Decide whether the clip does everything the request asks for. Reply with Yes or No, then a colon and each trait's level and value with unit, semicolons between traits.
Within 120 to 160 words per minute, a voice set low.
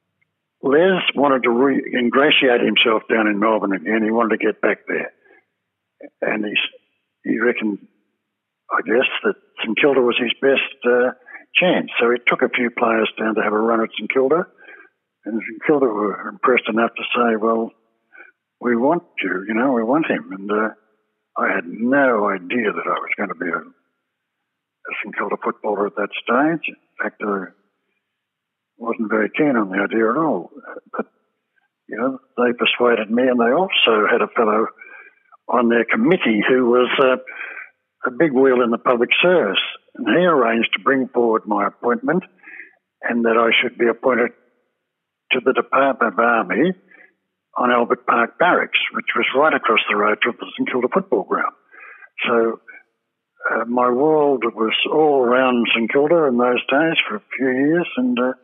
No: average, 175 wpm; low, 120 Hz